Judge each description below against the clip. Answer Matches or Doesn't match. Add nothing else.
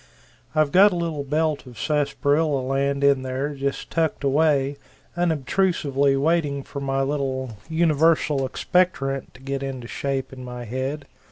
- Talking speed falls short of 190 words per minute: Matches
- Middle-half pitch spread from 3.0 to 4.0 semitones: Doesn't match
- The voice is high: Doesn't match